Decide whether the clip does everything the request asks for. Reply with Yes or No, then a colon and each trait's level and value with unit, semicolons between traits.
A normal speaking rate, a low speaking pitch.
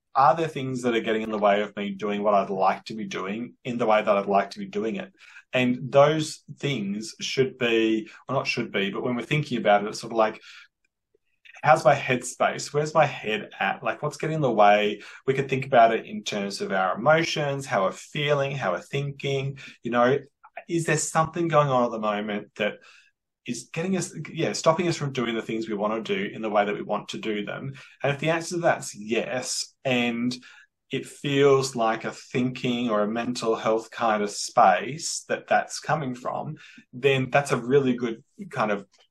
No: fast, 220 wpm; low, 125 Hz